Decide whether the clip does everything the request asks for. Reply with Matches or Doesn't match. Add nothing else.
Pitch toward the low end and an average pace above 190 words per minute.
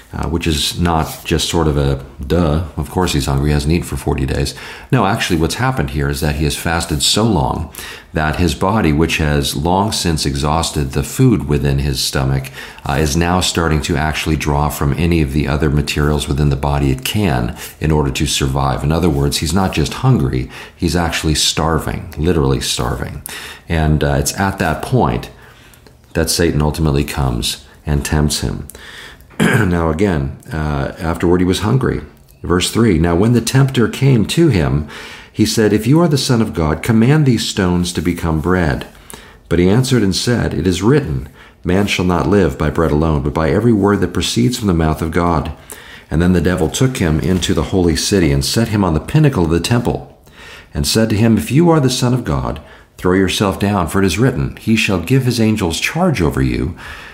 Matches